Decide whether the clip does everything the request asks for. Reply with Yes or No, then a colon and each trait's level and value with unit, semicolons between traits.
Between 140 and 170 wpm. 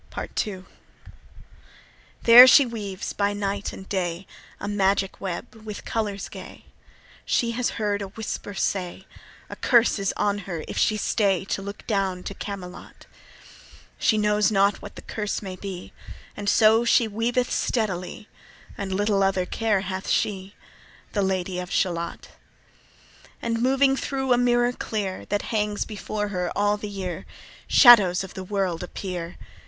Yes: average, 150 wpm